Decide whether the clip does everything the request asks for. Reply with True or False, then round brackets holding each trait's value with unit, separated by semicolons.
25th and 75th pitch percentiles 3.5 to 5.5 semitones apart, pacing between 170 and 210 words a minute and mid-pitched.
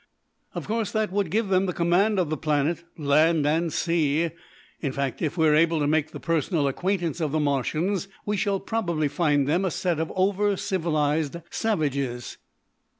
True (4.0 semitones; 180 wpm; 165 Hz)